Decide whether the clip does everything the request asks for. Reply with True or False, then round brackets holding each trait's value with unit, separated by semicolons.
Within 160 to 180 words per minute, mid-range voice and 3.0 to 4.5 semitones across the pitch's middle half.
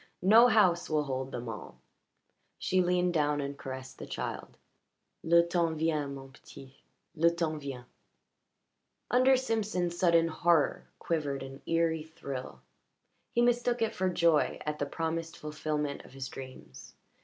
False (145 wpm; 160 Hz; 3.9 semitones)